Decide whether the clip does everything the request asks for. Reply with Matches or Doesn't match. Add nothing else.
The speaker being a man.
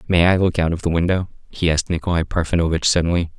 Matches